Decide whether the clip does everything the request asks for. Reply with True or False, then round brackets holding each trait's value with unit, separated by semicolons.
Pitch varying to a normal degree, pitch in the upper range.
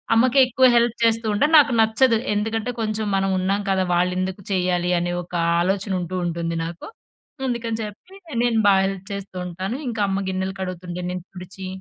True (3.6 semitones; 195 Hz)